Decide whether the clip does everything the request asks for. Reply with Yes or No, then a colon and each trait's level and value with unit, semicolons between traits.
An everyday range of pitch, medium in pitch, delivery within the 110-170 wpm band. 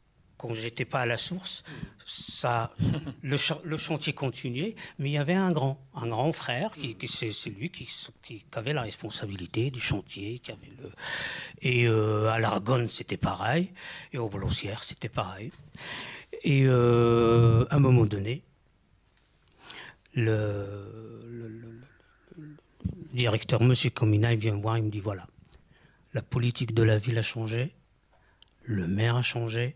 No: average, 3.6 semitones; low, 120 Hz; average, 165 wpm